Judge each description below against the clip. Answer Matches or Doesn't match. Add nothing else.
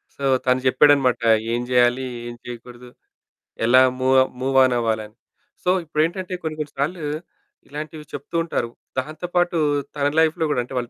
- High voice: Doesn't match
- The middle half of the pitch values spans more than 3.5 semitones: Matches